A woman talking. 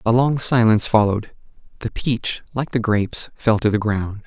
No: male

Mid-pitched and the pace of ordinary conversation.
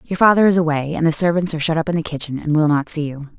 No: medium, 160 Hz; fast, 320 wpm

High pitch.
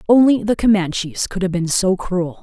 Yes: high, 195 Hz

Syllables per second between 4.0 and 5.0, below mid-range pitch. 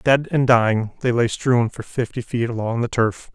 Yes: 4.7 syllables/s; low, 120 Hz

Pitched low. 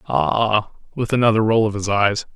Yes: low, 105 Hz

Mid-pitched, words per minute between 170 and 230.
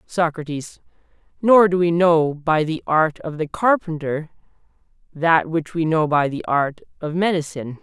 No: medium, 160 Hz; average, 155 wpm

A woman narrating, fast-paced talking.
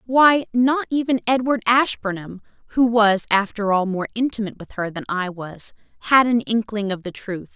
No: female; average, 175 wpm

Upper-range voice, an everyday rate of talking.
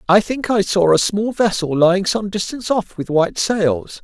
No: high, 195 Hz; fast, 210 wpm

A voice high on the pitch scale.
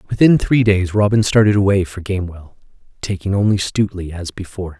No: very low, 95 Hz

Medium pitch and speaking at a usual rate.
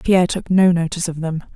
No: medium, 175 Hz; fast, 230 wpm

